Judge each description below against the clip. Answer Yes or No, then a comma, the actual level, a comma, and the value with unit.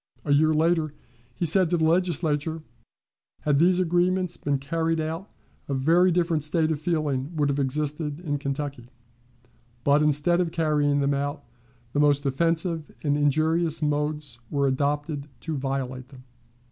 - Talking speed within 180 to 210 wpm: No, average, 150 wpm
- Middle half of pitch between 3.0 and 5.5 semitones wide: No, narrow, 2.5 semitones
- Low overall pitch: No, medium, 150 Hz